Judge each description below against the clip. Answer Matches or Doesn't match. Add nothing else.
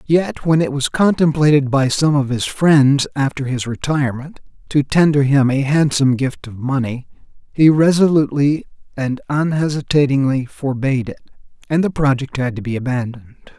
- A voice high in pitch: Doesn't match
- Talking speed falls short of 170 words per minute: Matches